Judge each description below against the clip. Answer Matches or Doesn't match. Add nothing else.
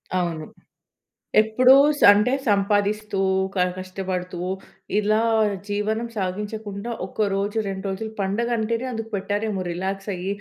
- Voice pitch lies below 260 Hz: Matches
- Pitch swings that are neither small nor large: Doesn't match